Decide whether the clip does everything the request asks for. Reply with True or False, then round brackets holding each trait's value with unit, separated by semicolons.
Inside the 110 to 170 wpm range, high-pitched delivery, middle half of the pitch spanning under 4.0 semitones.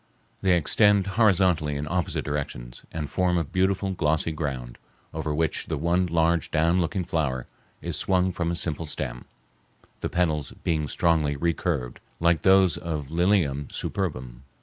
False (150 wpm; 80 Hz; 3.5 semitones)